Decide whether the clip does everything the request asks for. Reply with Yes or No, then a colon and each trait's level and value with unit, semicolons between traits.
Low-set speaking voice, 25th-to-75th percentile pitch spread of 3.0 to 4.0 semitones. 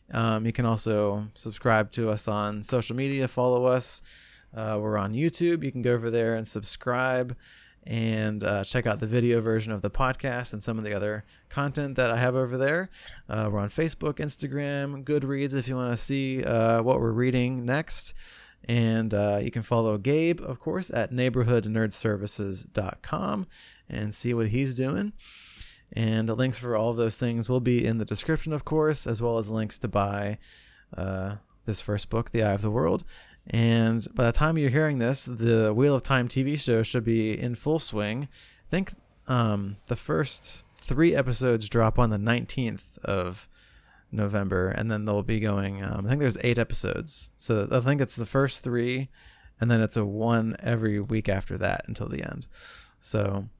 Yes: low, 115 Hz; average, 3.3 semitones